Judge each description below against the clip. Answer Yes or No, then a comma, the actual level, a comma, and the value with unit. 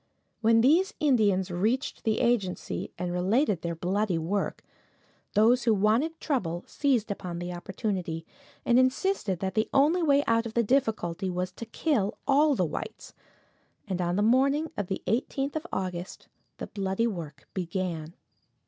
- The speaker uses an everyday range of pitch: No, wide, 6.1 semitones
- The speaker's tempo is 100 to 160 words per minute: Yes, average, 155 wpm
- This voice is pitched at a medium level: No, high, 210 Hz